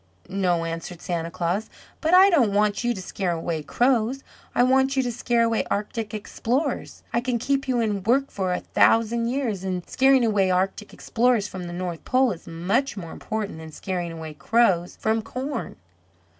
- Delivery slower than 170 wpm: No, average, 185 wpm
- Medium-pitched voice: No, high, 215 Hz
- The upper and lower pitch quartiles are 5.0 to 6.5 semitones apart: Yes, wide, 5.4 semitones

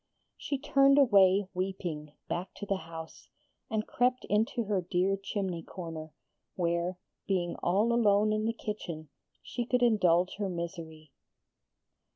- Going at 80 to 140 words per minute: Yes, slow, 135 wpm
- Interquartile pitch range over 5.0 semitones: No, average, 3.9 semitones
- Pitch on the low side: No, high, 190 Hz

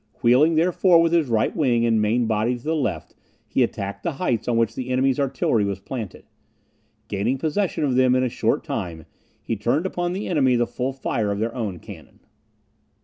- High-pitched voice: No, low, 125 Hz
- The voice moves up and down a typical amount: Yes, average, 5.0 semitones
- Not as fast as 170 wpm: No, average, 200 wpm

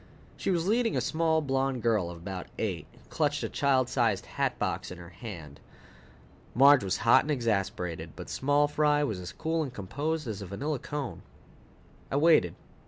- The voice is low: Yes, low, 130 Hz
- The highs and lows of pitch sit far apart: Yes, wide, 7.3 semitones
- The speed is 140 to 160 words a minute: No, average, 175 wpm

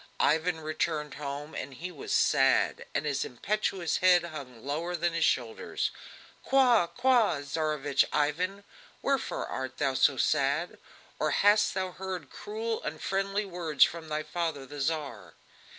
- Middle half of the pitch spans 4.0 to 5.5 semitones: Yes, average, 4.5 semitones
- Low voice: No, medium, 160 Hz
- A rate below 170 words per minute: Yes, average, 140 wpm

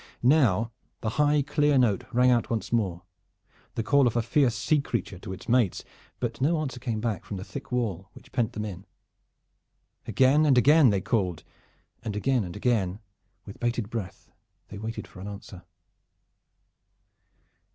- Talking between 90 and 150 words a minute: No, average, 165 wpm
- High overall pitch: No, low, 115 Hz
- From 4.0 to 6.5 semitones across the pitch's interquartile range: Yes, average, 4.3 semitones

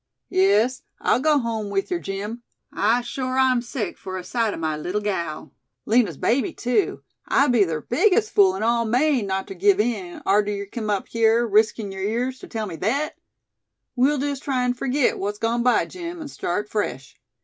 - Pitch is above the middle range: Yes, high, 225 Hz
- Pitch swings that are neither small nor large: Yes, average, 4.2 semitones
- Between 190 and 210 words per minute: Yes, average, 195 wpm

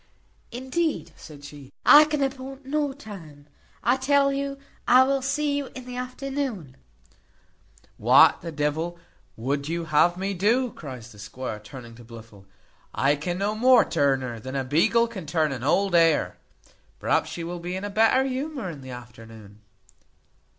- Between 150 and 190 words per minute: Yes, average, 165 wpm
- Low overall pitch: No, medium, 175 Hz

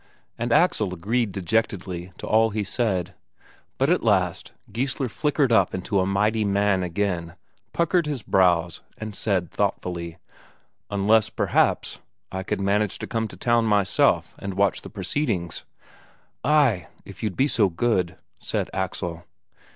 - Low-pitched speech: Yes, low, 100 Hz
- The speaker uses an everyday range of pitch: Yes, average, 3.8 semitones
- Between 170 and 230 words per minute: No, average, 145 wpm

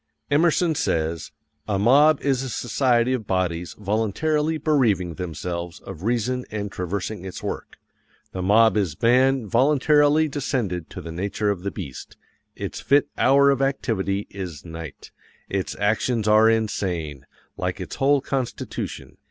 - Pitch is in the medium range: No, low, 110 Hz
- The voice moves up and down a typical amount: No, wide, 6.6 semitones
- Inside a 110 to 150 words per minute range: Yes, average, 145 wpm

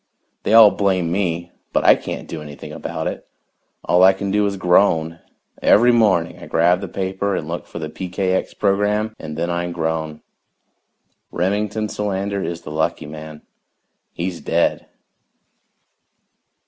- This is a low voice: Yes, very low, 90 Hz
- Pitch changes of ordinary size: Yes, average, 3.4 semitones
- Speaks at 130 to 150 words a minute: Yes, average, 145 wpm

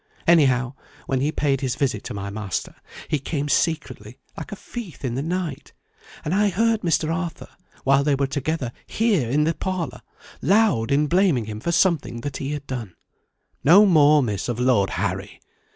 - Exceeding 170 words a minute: Yes, average, 180 wpm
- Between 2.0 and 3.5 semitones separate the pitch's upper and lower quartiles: No, wide, 5.4 semitones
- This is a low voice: No, medium, 145 Hz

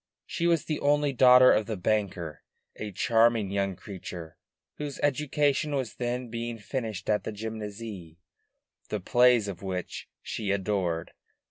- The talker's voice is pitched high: No, low, 110 Hz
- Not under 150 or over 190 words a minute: No, average, 140 wpm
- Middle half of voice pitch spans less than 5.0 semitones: Yes, average, 4.4 semitones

